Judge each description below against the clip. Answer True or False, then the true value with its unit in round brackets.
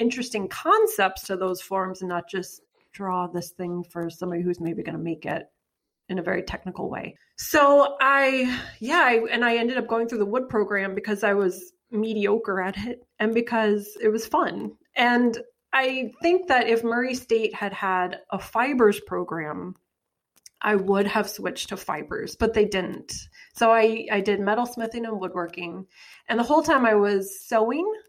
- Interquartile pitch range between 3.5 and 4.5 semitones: True (4.2 semitones)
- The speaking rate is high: False (180 wpm)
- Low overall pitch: False (215 Hz)